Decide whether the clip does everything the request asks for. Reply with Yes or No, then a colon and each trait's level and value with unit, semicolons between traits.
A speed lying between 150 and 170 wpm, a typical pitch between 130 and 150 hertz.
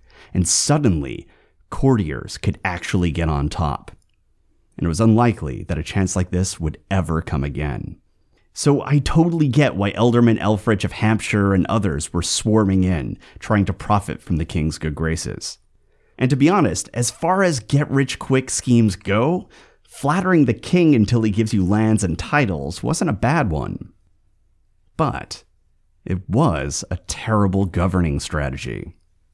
No: average, 155 wpm; low, 100 Hz